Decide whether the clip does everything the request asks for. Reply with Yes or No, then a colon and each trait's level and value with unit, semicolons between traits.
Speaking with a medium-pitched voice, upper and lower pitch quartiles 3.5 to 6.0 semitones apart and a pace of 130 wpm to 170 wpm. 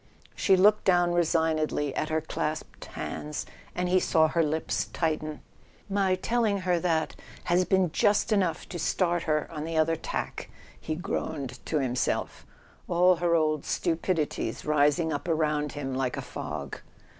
No: medium, 165 Hz; average, 2.8 semitones; average, 155 wpm